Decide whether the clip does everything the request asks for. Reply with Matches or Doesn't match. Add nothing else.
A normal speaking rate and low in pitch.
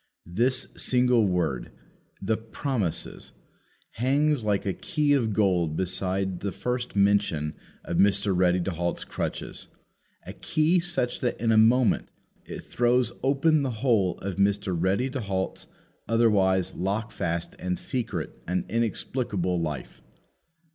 Doesn't match